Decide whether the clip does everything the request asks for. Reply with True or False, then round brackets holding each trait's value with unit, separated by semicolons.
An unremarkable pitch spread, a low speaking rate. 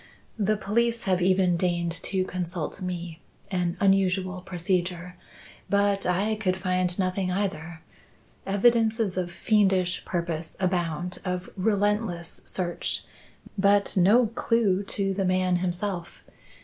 False (2.2 semitones; 115 wpm)